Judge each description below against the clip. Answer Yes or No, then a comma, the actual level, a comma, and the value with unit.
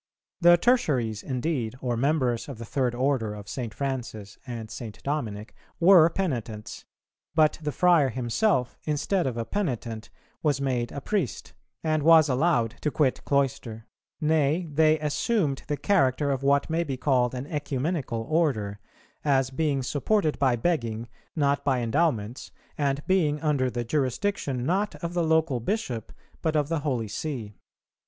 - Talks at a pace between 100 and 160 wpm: Yes, average, 150 wpm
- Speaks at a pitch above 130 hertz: Yes, medium, 140 Hz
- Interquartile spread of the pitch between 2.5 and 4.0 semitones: No, average, 4.7 semitones